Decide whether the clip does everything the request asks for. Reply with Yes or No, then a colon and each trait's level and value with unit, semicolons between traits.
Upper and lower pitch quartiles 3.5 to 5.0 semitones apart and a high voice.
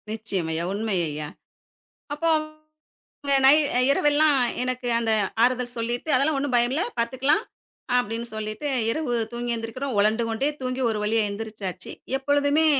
Yes: average, 4.1 semitones; high, 240 Hz